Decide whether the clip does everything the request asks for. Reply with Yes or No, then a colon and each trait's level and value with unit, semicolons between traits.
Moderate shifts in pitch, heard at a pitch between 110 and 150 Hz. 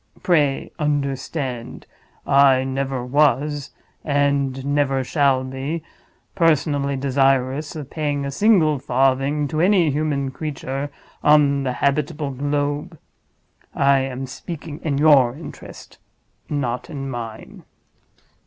No: narrow, 1.9 semitones; medium, 140 Hz